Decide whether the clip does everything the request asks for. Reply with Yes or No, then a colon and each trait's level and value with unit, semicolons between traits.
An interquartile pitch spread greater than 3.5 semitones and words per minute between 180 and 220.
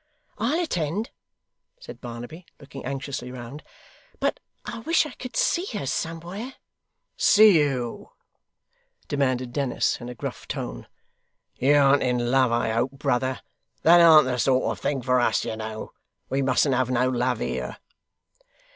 No: average, 4.8 semitones; average, 145 wpm